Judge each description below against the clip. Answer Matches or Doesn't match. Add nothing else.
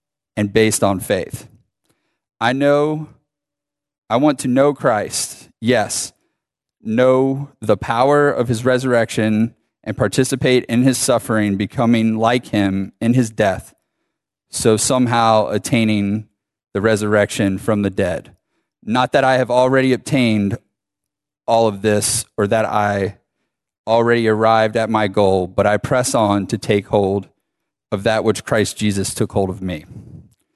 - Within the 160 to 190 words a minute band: Doesn't match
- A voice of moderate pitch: Doesn't match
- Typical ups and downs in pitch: Matches